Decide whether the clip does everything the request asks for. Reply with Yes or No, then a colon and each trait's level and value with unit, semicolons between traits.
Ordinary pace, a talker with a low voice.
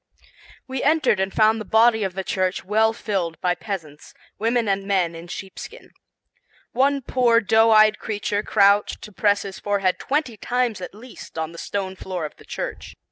No: average, 180 wpm; high, 205 Hz